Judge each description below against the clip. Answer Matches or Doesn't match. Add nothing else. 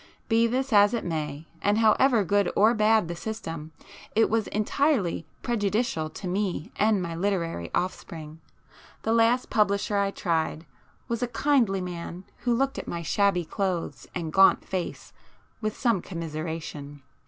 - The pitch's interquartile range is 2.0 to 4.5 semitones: Doesn't match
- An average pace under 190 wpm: Matches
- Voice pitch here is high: Matches